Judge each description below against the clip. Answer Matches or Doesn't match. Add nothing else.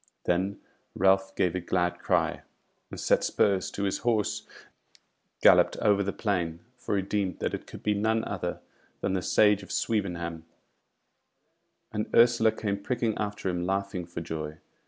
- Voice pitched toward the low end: Matches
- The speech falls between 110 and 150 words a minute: Doesn't match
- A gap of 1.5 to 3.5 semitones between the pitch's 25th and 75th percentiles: Matches